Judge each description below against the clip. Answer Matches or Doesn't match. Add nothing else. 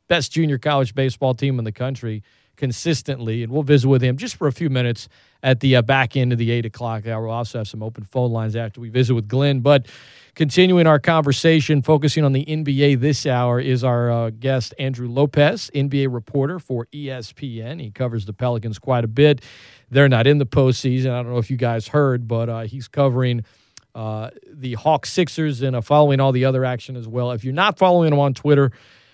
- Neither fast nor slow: Doesn't match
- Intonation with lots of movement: Doesn't match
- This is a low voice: Matches